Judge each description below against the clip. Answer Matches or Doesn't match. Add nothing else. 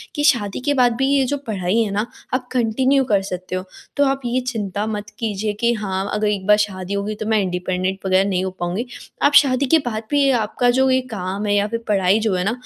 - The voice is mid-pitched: Doesn't match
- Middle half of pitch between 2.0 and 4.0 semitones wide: Doesn't match